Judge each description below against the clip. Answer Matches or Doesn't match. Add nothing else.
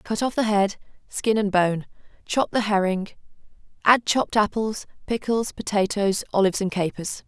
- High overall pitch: Matches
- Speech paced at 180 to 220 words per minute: Doesn't match